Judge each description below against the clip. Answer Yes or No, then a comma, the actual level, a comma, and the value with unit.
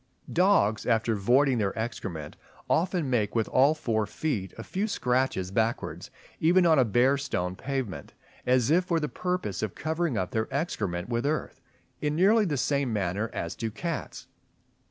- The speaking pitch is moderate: No, low, 125 Hz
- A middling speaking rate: Yes, average, 170 wpm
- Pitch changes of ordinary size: No, wide, 6.6 semitones